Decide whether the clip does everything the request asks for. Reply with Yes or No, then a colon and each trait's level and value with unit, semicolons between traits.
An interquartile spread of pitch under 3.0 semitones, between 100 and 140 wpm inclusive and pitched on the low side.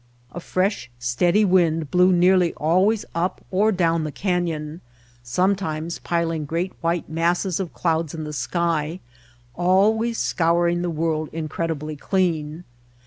No: narrow, 2.6 semitones; slow, 135 wpm; medium, 170 Hz